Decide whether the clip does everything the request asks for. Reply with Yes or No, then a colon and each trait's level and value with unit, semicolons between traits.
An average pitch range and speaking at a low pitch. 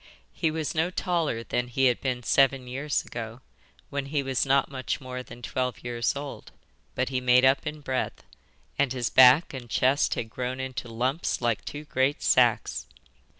No: narrow, 2.2 semitones; low, 130 Hz